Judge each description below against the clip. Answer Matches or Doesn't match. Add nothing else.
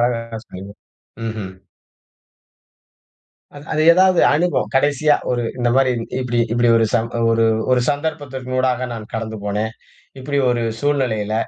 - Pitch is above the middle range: Doesn't match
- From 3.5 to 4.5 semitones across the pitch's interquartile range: Matches